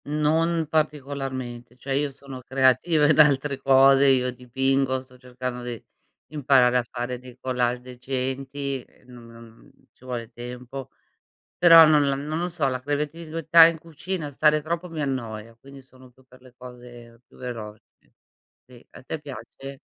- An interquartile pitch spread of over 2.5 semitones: Yes, average, 2.9 semitones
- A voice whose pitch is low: Yes, low, 130 Hz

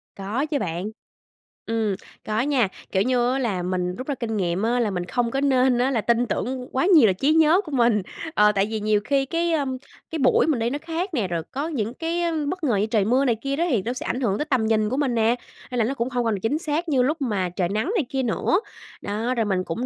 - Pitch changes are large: No, average, 4.7 semitones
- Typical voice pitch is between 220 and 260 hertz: Yes, high, 245 Hz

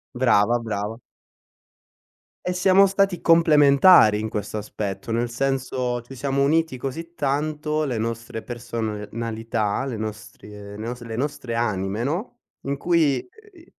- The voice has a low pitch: Yes, low, 125 Hz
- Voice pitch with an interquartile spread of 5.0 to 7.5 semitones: Yes, wide, 5.6 semitones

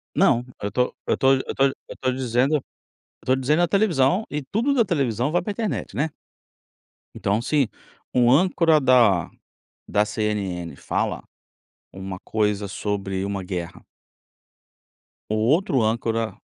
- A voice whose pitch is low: Yes, low, 125 Hz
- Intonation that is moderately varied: No, wide, 6.3 semitones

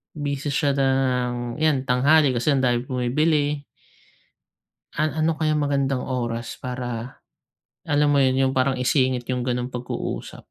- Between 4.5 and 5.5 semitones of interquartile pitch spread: No, narrow, 2.6 semitones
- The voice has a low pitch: Yes, low, 130 Hz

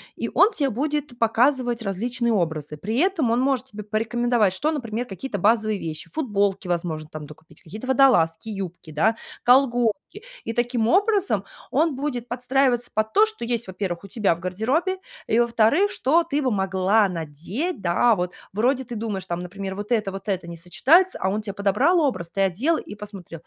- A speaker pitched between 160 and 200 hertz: No, high, 220 Hz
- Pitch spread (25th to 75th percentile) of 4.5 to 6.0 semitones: Yes, wide, 5.5 semitones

